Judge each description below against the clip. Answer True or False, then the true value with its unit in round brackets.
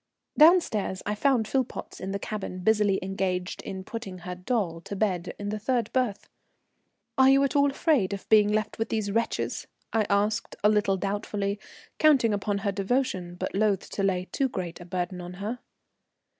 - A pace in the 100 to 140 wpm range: False (185 wpm)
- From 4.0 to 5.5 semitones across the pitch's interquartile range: False (3.2 semitones)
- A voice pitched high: True (205 Hz)